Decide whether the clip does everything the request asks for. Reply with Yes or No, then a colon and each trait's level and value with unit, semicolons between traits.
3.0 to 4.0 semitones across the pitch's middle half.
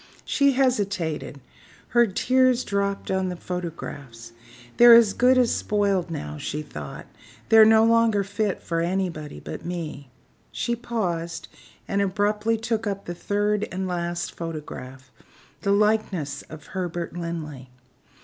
No: average, 4.7 semitones